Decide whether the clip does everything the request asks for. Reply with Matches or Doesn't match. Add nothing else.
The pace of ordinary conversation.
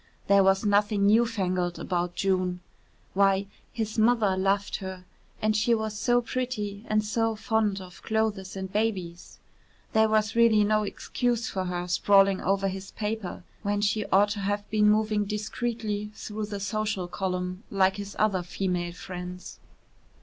Matches